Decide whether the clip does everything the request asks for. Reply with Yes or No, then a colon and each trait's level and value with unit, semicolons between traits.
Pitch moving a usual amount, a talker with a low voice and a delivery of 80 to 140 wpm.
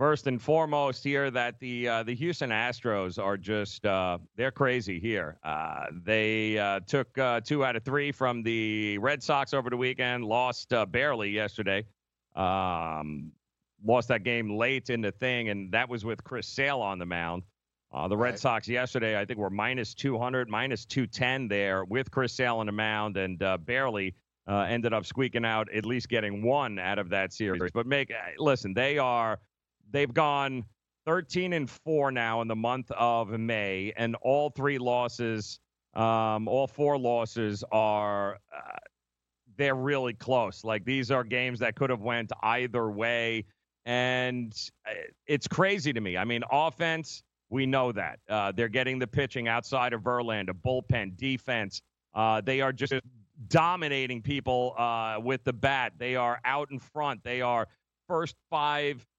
No: average, 3.7 semitones; low, 120 Hz; average, 170 wpm